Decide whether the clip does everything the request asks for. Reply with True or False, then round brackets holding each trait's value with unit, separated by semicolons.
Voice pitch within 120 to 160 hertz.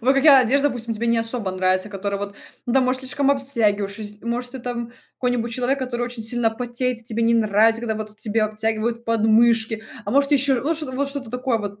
False (235 Hz)